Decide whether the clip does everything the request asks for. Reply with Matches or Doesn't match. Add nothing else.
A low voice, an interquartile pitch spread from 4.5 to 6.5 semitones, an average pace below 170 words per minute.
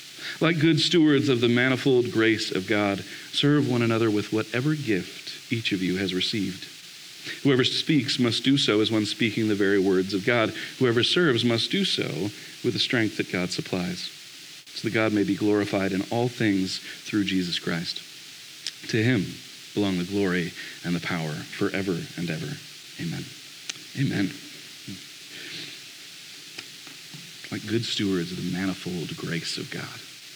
Matches